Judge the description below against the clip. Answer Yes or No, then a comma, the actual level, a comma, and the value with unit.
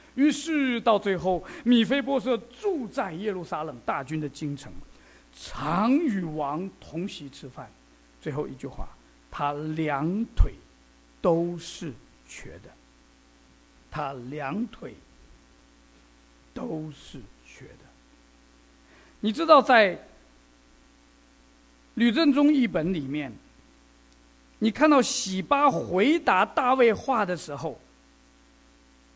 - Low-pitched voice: No, medium, 170 Hz